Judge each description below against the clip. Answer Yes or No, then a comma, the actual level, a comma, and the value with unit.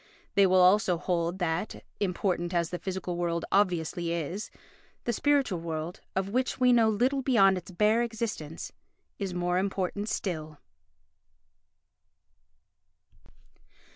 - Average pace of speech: No, slow, 120 wpm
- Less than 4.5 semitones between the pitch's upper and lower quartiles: Yes, average, 3.6 semitones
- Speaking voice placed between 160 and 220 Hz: Yes, medium, 185 Hz